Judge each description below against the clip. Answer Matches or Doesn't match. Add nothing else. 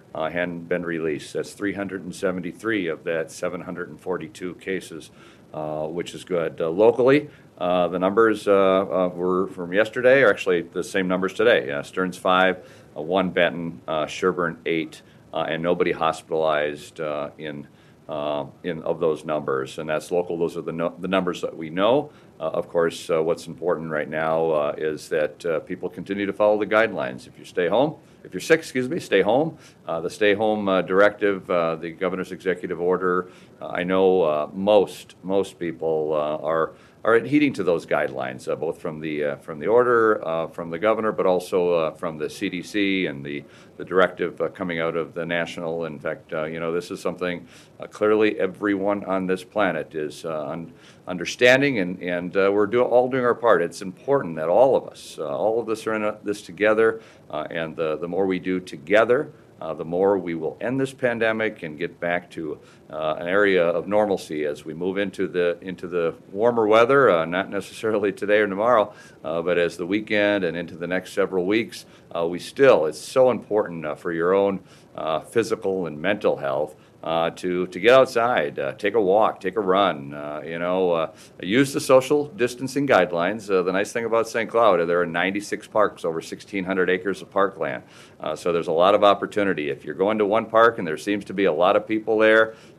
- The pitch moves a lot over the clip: Doesn't match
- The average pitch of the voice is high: Doesn't match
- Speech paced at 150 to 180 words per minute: Doesn't match